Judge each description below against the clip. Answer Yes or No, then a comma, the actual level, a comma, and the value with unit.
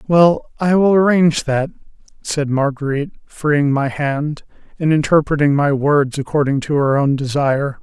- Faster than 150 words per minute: No, average, 145 wpm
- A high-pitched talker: No, medium, 145 Hz